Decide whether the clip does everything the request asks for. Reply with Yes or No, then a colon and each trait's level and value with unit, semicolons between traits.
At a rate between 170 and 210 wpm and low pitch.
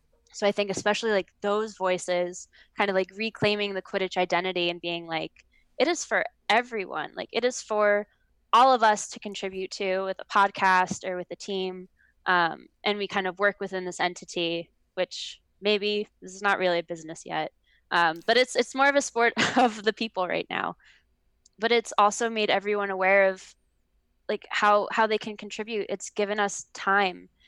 No: average, 190 wpm; high, 200 Hz